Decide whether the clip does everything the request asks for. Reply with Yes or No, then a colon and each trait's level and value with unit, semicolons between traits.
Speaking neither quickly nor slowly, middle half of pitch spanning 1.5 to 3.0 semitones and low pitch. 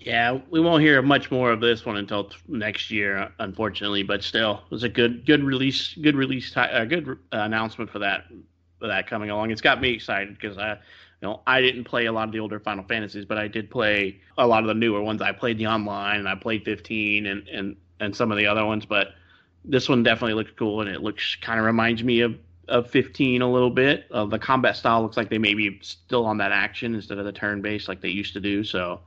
No: fast, 245 wpm; average, 2.7 semitones; low, 110 Hz